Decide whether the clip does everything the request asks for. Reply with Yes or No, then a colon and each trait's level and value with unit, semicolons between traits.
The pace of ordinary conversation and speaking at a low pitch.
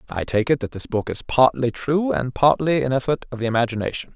No: fast, 230 wpm; low, 125 Hz